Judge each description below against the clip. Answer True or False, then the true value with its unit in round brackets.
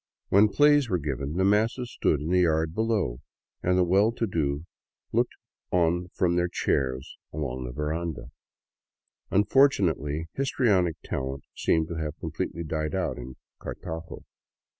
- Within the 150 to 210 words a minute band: False (140 wpm)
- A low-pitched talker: True (85 Hz)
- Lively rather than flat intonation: False (4.9 semitones)